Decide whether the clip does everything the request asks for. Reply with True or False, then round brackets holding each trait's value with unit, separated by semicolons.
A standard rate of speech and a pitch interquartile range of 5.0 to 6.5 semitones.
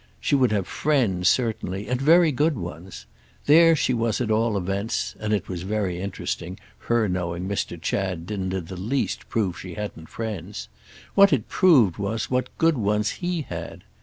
True (165 wpm; 5.4 semitones)